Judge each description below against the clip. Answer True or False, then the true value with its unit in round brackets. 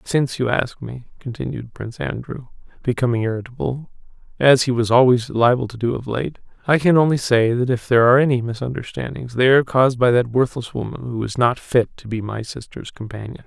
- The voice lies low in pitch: True (125 Hz)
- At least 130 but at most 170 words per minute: False (185 wpm)